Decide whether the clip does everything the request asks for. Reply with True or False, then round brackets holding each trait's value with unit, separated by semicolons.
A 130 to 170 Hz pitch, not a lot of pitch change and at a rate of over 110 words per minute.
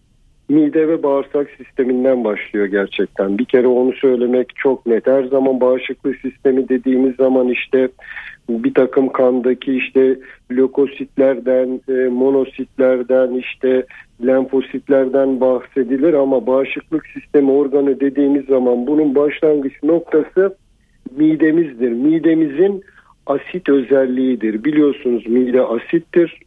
False (135 Hz; 2.1 semitones; 100 wpm)